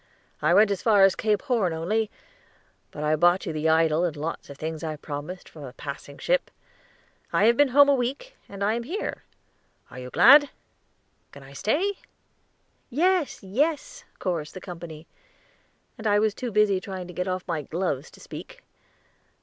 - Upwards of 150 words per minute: Yes, average, 180 wpm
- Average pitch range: No, wide, 6.9 semitones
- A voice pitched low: No, high, 190 Hz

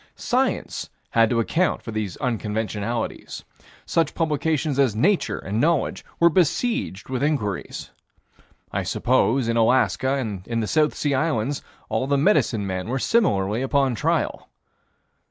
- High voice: No, low, 130 Hz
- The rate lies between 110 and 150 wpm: Yes, slow, 135 wpm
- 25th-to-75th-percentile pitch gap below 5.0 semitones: No, wide, 5.4 semitones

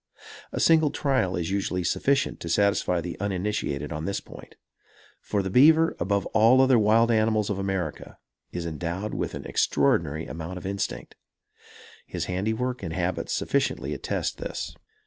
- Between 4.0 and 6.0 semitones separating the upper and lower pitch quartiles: Yes, average, 4.3 semitones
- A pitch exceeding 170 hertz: No, low, 100 Hz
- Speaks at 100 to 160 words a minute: Yes, average, 150 wpm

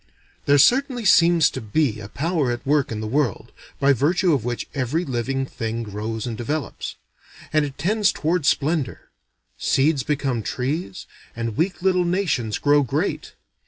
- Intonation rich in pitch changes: Yes, wide, 5.7 semitones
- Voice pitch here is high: No, medium, 140 Hz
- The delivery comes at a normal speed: Yes, average, 160 wpm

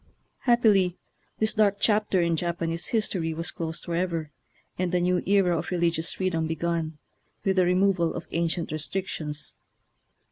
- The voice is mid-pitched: Yes, medium, 175 Hz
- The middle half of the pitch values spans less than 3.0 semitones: Yes, narrow, 2.5 semitones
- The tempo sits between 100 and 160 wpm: Yes, average, 140 wpm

